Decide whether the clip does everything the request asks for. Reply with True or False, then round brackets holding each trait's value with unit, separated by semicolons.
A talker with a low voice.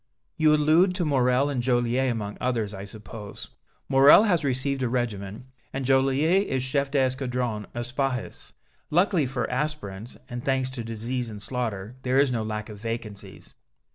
True (125 Hz)